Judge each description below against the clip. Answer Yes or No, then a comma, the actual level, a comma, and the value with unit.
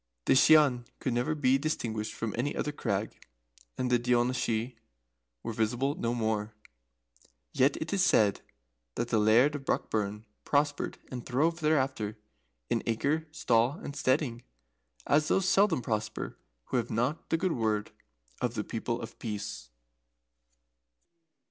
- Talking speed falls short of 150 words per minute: Yes, average, 140 wpm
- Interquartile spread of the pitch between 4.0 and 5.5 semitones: Yes, average, 4.6 semitones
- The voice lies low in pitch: Yes, low, 125 Hz